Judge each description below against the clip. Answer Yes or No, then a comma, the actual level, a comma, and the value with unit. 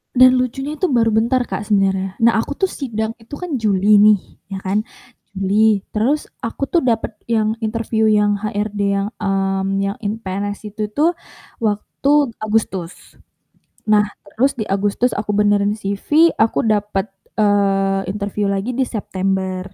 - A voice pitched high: Yes, high, 210 Hz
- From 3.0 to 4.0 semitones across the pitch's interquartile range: No, narrow, 2.5 semitones